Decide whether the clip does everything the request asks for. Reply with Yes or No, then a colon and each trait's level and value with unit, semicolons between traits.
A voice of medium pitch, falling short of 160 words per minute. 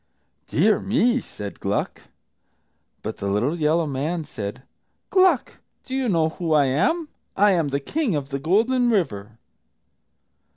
Yes: medium, 165 Hz; average, 140 wpm